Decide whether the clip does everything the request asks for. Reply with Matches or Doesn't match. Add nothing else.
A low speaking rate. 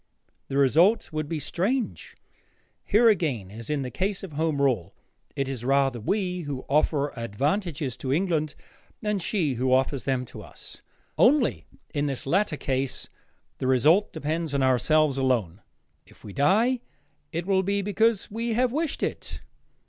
Doesn't match